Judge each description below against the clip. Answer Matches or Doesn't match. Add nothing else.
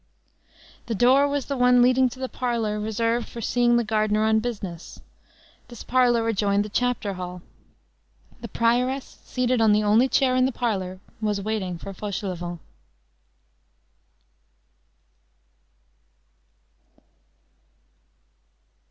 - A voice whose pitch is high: Matches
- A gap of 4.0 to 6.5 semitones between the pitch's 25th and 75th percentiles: Doesn't match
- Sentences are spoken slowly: Matches